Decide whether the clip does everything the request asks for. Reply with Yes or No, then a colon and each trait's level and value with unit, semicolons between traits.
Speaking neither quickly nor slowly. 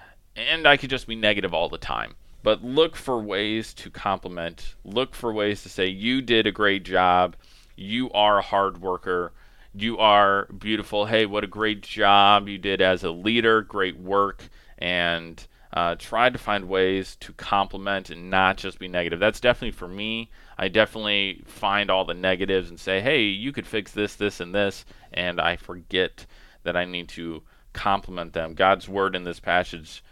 Yes: average, 185 wpm